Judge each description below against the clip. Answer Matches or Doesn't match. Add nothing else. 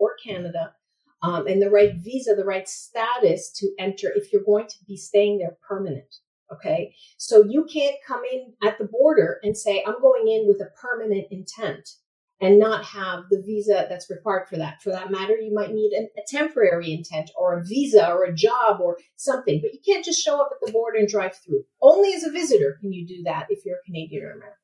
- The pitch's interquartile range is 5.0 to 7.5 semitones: Matches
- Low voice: Doesn't match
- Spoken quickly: Matches